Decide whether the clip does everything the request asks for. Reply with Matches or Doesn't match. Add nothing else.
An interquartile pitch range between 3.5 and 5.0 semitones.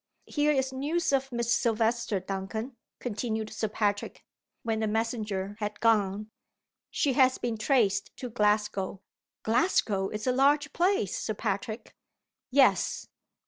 Matches